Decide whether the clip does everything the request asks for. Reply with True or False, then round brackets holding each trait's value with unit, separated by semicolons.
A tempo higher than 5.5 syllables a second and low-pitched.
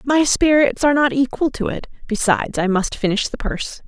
False (5.7 syllables/s; 245 Hz)